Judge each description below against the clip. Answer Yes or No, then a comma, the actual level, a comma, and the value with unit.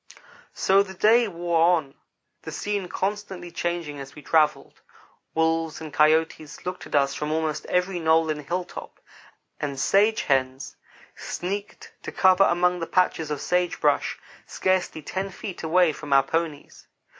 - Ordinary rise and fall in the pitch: Yes, average, 3.3 semitones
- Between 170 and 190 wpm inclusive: No, average, 150 wpm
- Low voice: No, medium, 165 Hz